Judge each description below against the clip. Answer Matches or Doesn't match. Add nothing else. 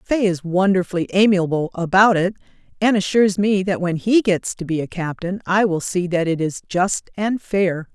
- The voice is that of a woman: Matches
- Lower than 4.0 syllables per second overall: Doesn't match